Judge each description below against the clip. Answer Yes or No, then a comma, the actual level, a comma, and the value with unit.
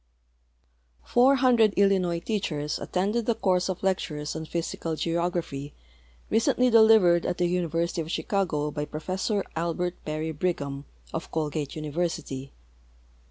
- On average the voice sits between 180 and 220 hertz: No, medium, 170 Hz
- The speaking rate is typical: No, slow, 120 wpm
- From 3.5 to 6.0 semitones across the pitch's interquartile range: Yes, average, 3.9 semitones